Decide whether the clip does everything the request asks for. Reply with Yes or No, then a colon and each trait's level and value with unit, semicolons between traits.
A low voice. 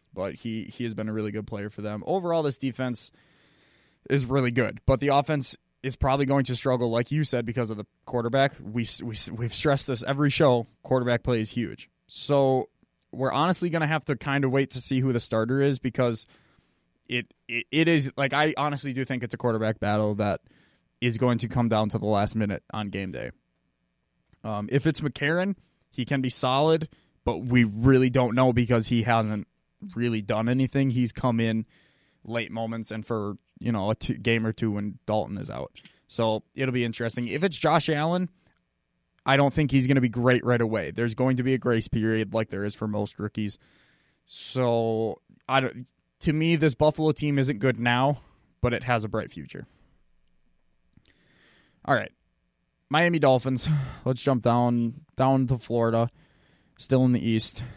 Yes: low, 125 Hz